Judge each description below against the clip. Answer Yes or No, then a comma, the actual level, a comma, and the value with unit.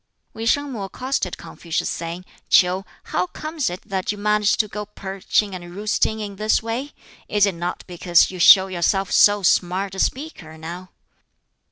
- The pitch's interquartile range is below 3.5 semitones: Yes, average, 2.8 semitones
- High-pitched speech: Yes, high, 195 Hz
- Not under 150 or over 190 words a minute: Yes, average, 170 wpm